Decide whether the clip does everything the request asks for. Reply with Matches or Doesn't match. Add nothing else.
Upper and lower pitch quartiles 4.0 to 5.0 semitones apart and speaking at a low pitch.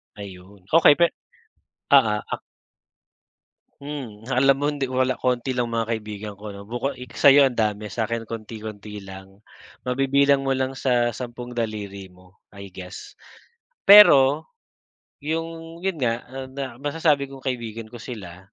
Matches